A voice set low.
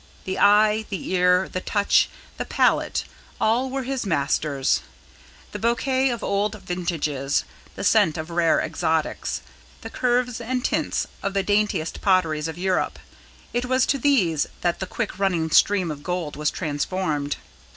No: medium, 185 Hz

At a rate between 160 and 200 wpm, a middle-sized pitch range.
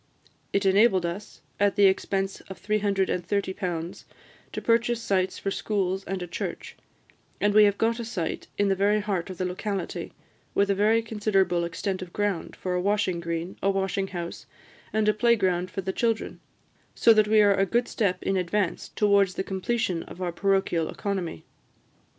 No: average, 180 wpm; narrow, 2.3 semitones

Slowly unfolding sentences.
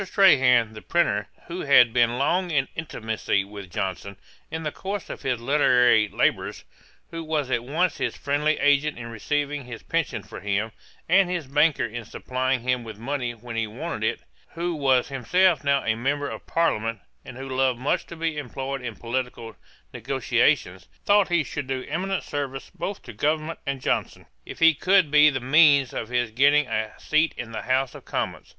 No: average, 185 wpm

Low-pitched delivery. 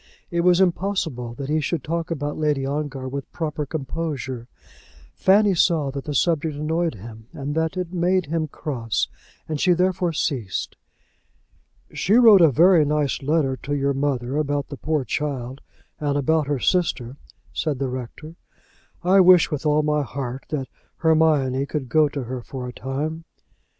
No: medium, 150 Hz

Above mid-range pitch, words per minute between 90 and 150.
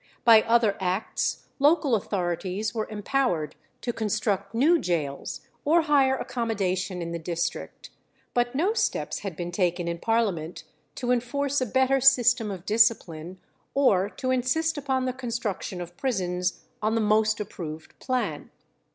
Yes: high, 220 Hz; average, 145 wpm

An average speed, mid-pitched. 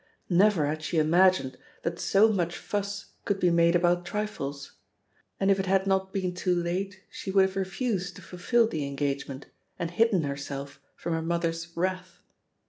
Yes: average, 170 wpm; medium, 180 Hz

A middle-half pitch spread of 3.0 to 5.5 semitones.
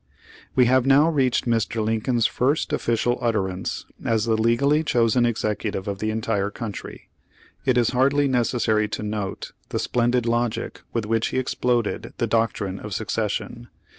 No: narrow, 2.4 semitones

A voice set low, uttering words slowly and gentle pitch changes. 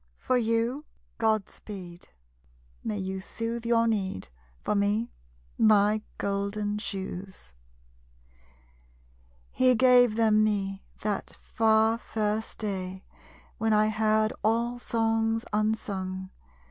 No: high, 215 Hz; slow, 95 wpm; narrow, 2.1 semitones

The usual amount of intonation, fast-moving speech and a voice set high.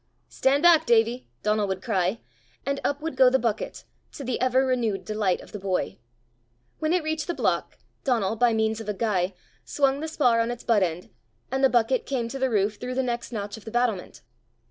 Yes: average, 3.9 semitones; fast, 210 wpm; high, 235 Hz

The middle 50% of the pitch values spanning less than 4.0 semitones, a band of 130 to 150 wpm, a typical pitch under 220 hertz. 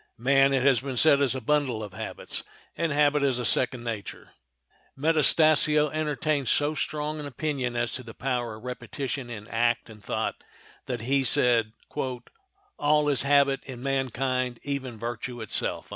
No: average, 3.3 semitones; average, 160 wpm; low, 135 Hz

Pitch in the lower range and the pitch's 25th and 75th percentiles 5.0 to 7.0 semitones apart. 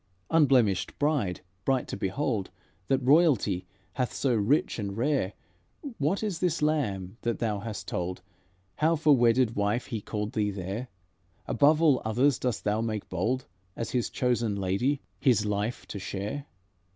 Yes: low, 115 Hz; wide, 5.4 semitones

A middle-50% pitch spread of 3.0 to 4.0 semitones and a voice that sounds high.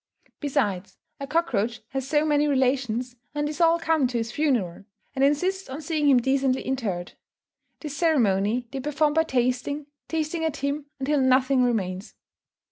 Yes: average, 3.4 semitones; very high, 270 Hz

